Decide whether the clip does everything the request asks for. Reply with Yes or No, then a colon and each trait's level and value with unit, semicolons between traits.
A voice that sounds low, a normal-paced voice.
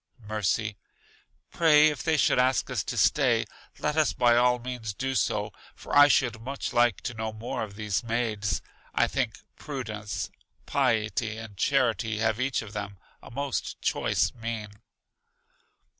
Yes: low, 115 Hz; average, 155 wpm